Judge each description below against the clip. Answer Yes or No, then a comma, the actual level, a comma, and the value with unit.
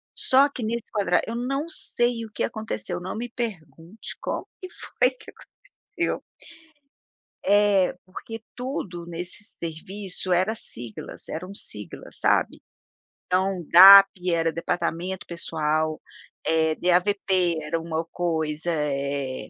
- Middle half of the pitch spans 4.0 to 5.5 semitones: Yes, average, 4.6 semitones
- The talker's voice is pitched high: No, medium, 180 Hz